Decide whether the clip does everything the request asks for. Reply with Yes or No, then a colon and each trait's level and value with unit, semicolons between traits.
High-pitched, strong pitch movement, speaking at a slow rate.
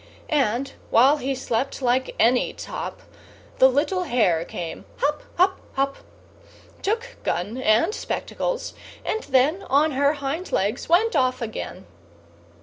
No: very high, 270 Hz; average, 4.4 semitones; slow, 130 wpm